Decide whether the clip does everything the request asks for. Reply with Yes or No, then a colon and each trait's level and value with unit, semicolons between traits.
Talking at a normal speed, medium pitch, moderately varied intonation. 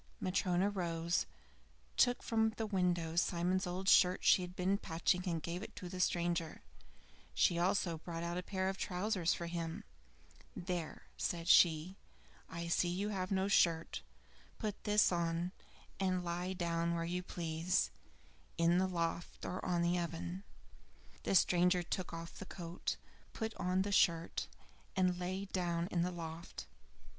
No: average, 155 wpm; medium, 180 Hz; narrow, 1.7 semitones